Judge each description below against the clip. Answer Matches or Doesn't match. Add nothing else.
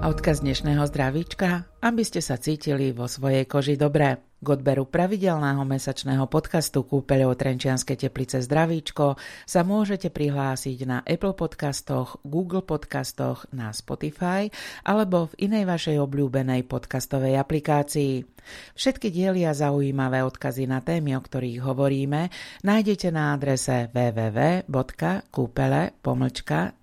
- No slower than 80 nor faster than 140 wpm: Matches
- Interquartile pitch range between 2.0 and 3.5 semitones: Doesn't match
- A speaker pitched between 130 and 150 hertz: Matches